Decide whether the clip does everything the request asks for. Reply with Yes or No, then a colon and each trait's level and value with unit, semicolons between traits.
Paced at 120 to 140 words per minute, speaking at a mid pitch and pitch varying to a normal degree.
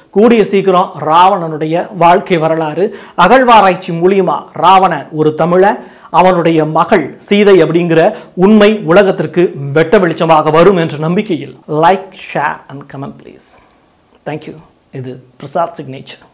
No: average, 110 wpm; medium, 175 Hz; average, 3.6 semitones